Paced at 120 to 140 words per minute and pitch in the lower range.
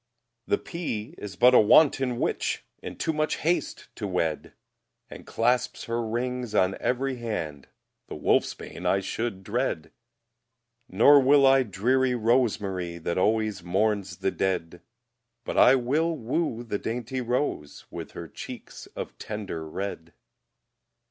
Yes: slow, 135 wpm; low, 115 Hz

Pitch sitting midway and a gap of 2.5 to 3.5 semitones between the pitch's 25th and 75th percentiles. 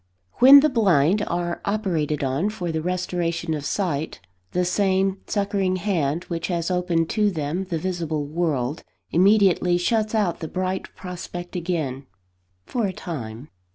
Yes: medium, 175 Hz; average, 3.2 semitones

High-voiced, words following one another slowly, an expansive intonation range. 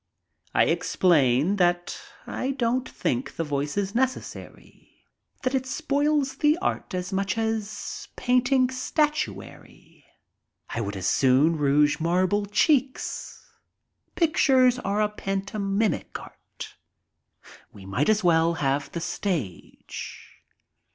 Yes: high, 200 Hz; slow, 110 wpm; wide, 8.0 semitones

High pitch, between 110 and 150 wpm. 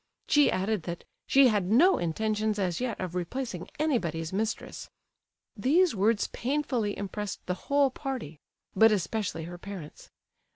Yes: high, 210 Hz; slow, 135 wpm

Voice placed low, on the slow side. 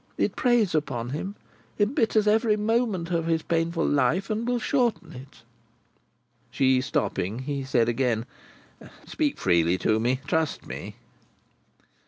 No: medium, 160 Hz; slow, 130 wpm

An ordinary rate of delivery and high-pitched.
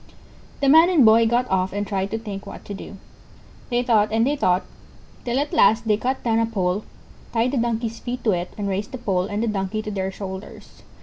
No: fast, 230 wpm; high, 220 Hz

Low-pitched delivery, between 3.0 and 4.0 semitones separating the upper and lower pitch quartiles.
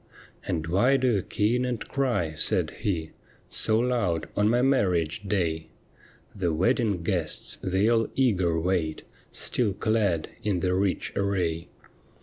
No: very low, 95 Hz; average, 5.2 semitones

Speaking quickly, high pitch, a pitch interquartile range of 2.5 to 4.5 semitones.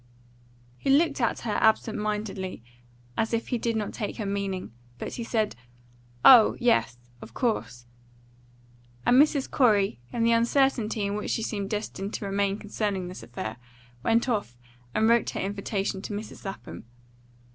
No: average, 155 wpm; high, 210 Hz; average, 2.9 semitones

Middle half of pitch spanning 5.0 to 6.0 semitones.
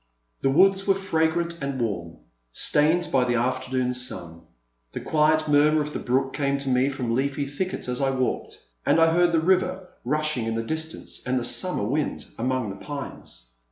No: average, 4.2 semitones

